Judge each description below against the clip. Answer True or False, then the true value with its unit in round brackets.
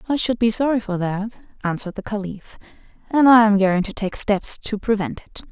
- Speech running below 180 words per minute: False (205 wpm)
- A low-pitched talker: False (215 Hz)